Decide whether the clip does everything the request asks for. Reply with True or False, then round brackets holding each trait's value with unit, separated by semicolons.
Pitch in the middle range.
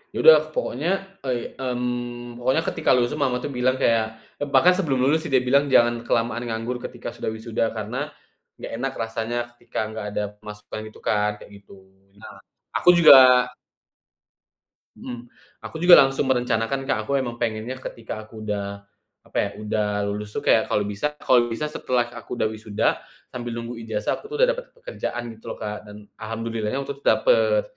False (120 Hz)